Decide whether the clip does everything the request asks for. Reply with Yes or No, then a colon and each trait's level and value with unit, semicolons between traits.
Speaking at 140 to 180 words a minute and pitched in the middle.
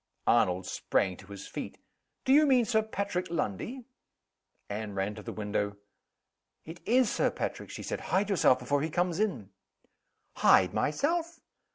Yes: average, 155 wpm; medium, 160 Hz